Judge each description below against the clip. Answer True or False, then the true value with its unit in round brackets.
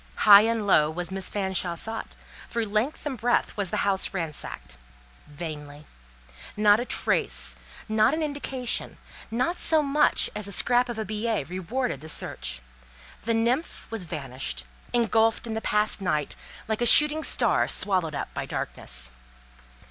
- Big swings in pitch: True (5.8 semitones)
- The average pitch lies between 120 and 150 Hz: False (210 Hz)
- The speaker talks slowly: False (155 wpm)